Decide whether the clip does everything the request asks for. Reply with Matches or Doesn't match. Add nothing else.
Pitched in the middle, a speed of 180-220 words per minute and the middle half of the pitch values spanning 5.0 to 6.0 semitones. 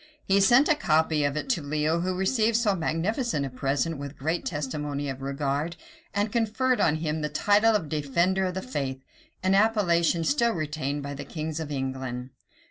Matches